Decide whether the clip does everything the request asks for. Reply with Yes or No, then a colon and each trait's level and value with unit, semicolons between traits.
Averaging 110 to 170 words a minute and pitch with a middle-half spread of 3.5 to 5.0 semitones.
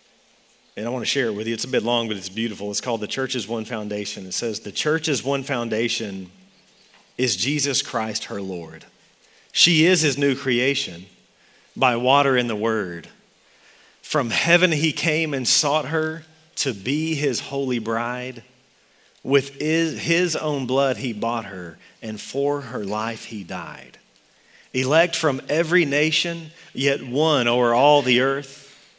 Yes: average, 160 wpm; average, 4.4 semitones